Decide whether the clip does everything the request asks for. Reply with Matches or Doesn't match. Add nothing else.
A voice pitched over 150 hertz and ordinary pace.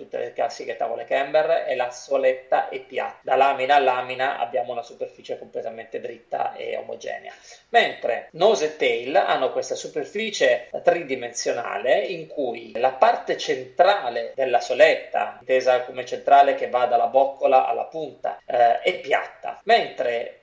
Matches